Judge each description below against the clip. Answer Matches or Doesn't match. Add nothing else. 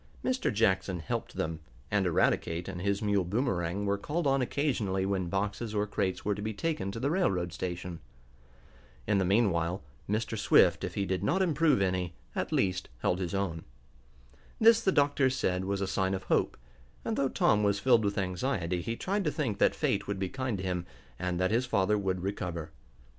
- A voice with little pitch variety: Doesn't match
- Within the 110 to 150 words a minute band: Doesn't match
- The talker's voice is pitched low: Matches